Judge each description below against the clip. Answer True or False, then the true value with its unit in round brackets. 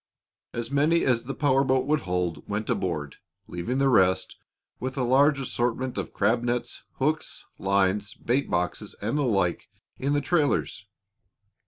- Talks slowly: False (155 wpm)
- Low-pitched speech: True (120 Hz)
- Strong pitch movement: True (5.8 semitones)